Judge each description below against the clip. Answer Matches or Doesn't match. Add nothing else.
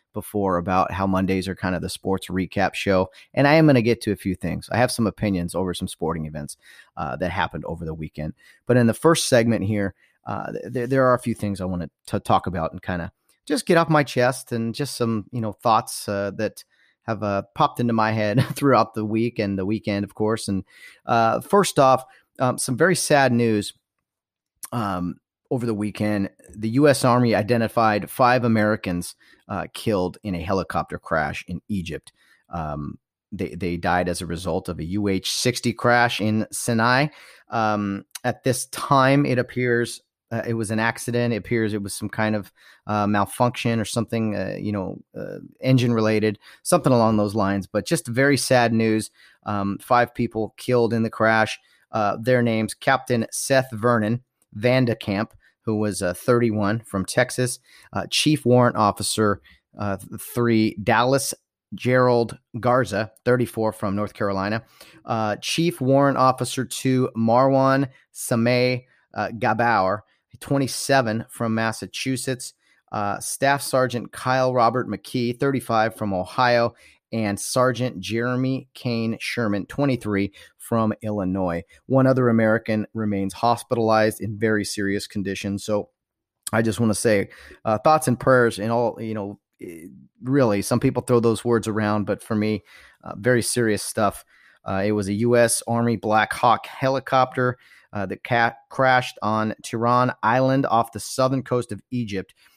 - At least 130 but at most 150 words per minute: Doesn't match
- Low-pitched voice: Matches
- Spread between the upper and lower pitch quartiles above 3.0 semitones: Matches